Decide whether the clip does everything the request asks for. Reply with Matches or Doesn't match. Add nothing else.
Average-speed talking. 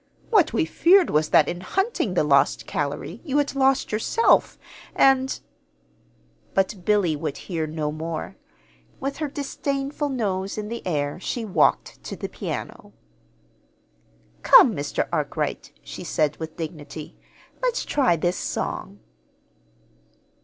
Doesn't match